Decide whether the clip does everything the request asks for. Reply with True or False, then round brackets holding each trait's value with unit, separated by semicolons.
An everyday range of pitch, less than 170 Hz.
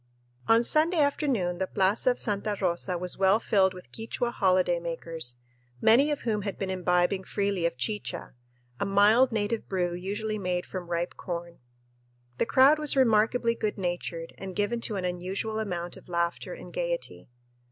False (4.2 semitones; 195 Hz)